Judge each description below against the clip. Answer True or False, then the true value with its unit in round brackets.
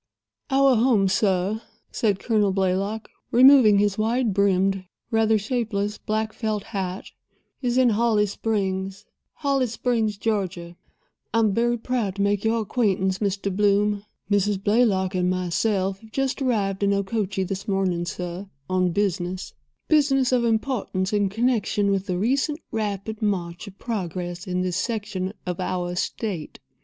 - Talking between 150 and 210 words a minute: False (140 wpm)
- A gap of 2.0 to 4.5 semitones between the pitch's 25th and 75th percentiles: True (2.9 semitones)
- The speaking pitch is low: False (205 Hz)